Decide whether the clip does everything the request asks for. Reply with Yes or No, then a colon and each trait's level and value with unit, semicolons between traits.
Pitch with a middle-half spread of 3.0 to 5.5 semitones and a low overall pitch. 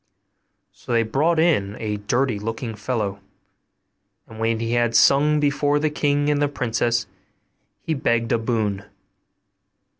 Yes: average, 4.4 semitones; low, 120 Hz